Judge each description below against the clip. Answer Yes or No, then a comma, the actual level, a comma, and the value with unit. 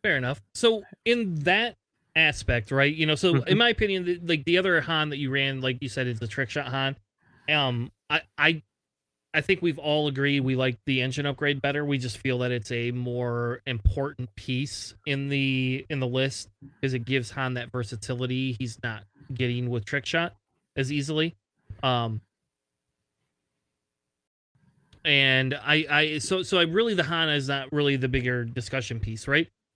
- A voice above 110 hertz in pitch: Yes, low, 135 Hz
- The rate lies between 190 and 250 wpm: No, average, 180 wpm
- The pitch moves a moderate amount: Yes, average, 3.5 semitones